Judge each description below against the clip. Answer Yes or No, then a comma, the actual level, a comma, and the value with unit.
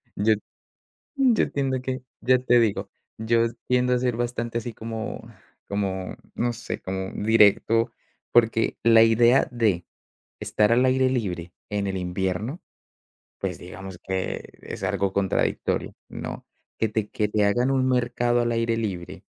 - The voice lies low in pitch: Yes, low, 115 Hz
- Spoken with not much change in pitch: No, average, 3.4 semitones